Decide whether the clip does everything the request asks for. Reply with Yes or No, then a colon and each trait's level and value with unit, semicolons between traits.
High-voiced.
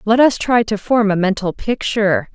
Yes: high, 210 Hz